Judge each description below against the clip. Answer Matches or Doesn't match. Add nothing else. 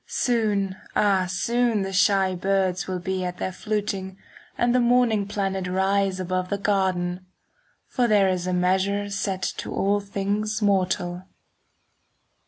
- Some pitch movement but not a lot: Doesn't match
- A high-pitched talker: Matches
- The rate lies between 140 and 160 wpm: Matches